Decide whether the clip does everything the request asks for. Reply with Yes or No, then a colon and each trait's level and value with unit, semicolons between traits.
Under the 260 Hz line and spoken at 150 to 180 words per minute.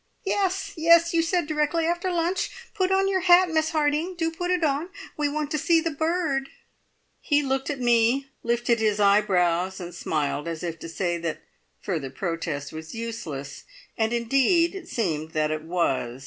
No: very high, 270 Hz; average, 175 wpm